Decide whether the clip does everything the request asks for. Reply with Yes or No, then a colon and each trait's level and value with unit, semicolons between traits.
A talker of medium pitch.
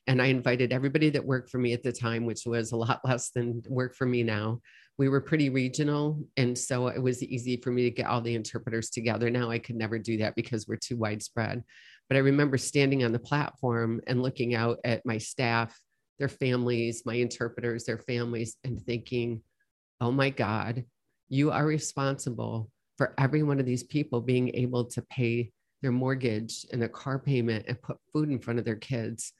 No: low, 120 Hz